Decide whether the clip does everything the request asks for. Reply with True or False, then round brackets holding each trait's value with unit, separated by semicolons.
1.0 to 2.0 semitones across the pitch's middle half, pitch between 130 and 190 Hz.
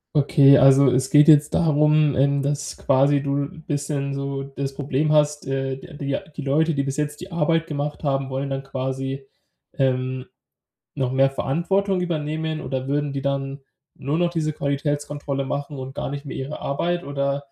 True (1.6 semitones; 140 Hz)